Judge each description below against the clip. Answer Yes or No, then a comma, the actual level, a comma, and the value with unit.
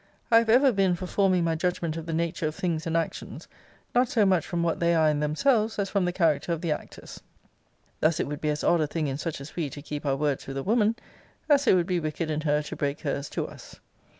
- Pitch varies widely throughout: No, average, 3.8 semitones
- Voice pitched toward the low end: No, medium, 165 Hz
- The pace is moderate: No, fast, 260 wpm